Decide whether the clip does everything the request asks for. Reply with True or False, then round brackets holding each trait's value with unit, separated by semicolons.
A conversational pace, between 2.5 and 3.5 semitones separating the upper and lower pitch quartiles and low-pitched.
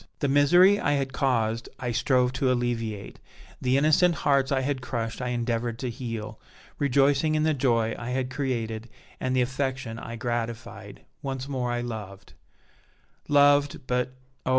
True (155 wpm; 2.9 semitones; 125 Hz)